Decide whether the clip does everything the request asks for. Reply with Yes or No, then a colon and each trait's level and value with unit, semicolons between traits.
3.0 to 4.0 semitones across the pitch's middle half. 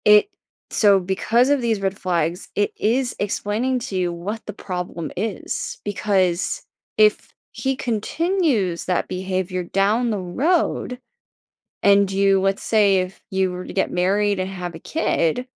Yes: average, 3.3 semitones